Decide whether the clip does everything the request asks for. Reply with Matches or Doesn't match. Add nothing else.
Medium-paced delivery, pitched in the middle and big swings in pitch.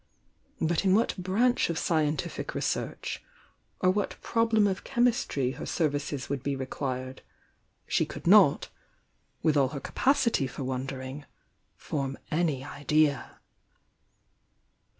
Doesn't match